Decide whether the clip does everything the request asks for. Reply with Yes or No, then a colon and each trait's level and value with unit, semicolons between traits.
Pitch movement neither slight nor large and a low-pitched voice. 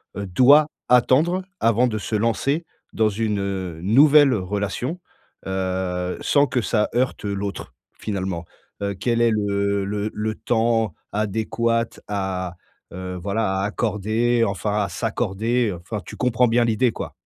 Yes: average, 3.2 semitones; low, 110 Hz